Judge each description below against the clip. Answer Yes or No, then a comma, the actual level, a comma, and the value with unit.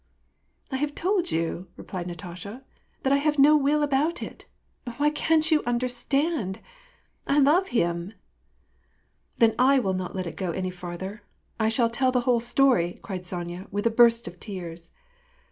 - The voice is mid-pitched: No, high, 230 Hz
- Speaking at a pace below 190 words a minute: Yes, average, 180 wpm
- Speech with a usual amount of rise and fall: No, wide, 7.3 semitones